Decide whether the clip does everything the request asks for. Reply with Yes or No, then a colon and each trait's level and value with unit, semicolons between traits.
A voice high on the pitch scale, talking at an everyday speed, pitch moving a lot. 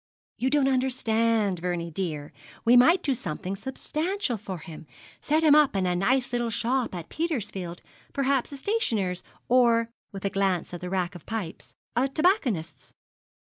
Yes: high, 230 Hz; average, 160 wpm; wide, 6.6 semitones